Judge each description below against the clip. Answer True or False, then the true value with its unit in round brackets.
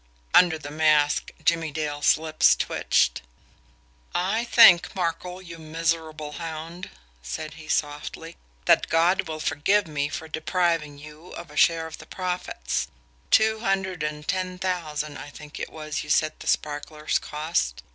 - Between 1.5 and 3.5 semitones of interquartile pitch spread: True (2.8 semitones)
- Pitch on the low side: False (160 Hz)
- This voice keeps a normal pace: True (145 wpm)